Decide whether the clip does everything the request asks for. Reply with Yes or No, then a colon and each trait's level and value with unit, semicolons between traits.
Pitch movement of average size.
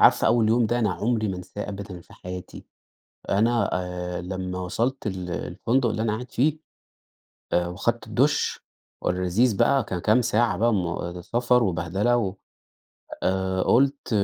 Yes: average, 4.6 semitones